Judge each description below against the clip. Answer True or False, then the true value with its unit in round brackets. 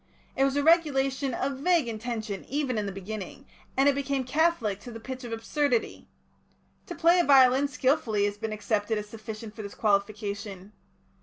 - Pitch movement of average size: True (4.7 semitones)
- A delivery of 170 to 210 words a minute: True (175 wpm)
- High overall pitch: True (240 Hz)